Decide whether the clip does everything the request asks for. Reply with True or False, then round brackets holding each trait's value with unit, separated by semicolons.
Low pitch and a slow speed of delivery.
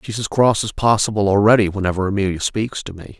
False (105 Hz; 205 wpm)